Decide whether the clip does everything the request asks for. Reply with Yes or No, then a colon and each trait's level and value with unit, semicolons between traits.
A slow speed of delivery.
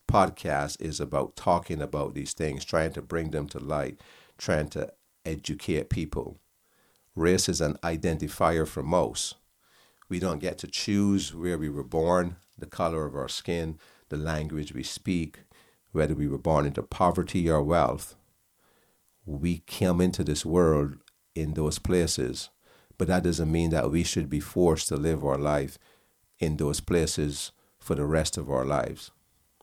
No: average, 160 wpm